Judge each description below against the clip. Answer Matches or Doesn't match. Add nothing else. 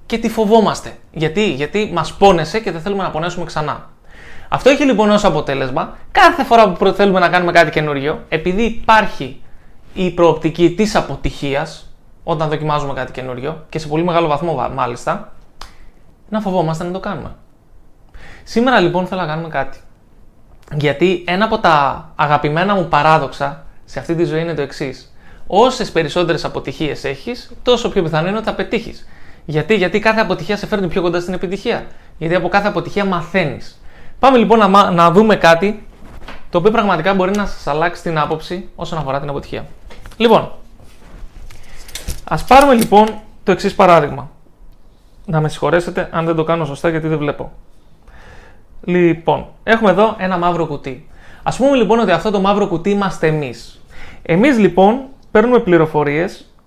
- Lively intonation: Doesn't match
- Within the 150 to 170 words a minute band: Matches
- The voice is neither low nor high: Matches